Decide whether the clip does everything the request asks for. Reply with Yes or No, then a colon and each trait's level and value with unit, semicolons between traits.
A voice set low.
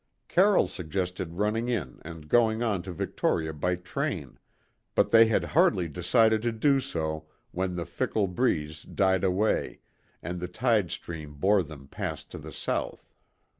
Yes: very low, 90 Hz